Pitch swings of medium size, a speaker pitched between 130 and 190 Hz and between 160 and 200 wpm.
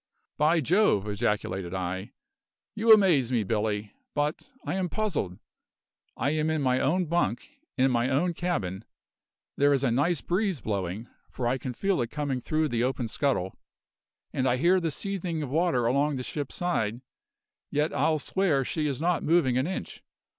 No: wide, 6.2 semitones; medium, 140 Hz; average, 170 wpm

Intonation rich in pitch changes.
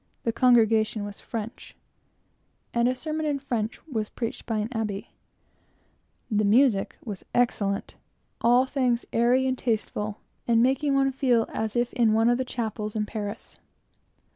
No: average, 2.8 semitones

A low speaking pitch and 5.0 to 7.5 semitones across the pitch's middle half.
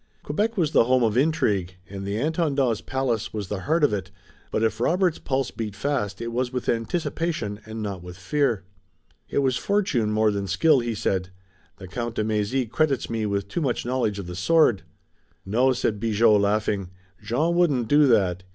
Yes: low, 115 Hz; wide, 5.4 semitones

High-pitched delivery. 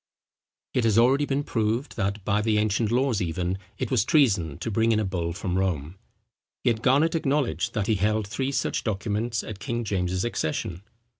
No: low, 110 Hz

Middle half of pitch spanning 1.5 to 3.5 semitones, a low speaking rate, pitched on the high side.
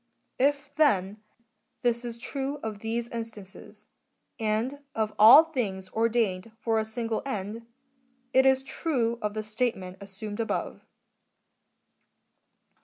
Yes: average, 2.8 semitones; slow, 120 wpm; high, 225 Hz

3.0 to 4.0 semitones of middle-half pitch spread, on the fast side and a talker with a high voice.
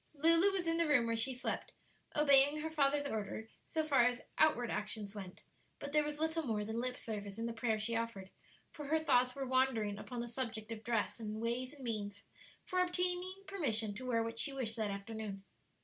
No: average, 5.1 semitones; fast, 210 wpm; high, 245 Hz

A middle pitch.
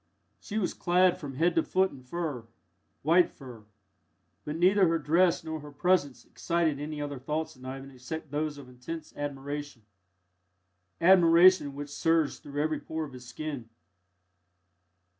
Yes: medium, 150 Hz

